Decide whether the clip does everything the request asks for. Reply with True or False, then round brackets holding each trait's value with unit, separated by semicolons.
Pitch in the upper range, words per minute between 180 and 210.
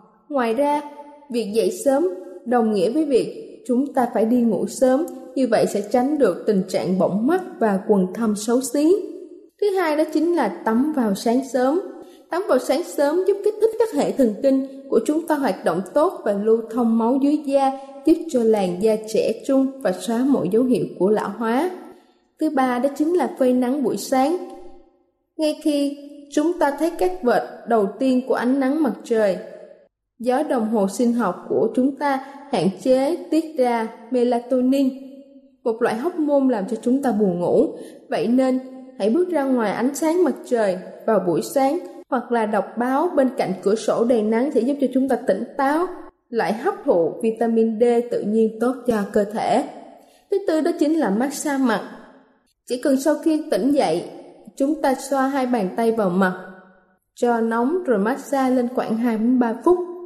True (260 Hz; 190 wpm)